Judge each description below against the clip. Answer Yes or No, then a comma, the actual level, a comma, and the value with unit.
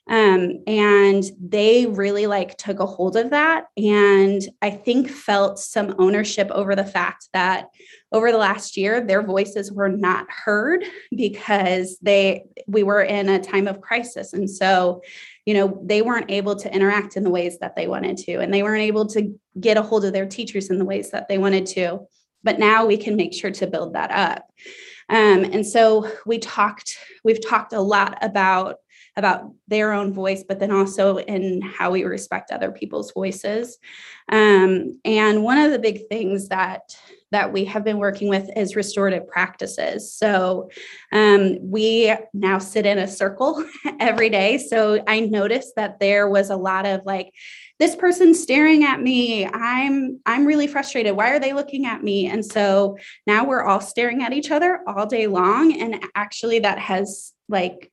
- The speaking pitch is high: Yes, high, 205 Hz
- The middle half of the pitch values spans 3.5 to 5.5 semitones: No, narrow, 2.6 semitones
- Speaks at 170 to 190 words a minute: Yes, average, 180 wpm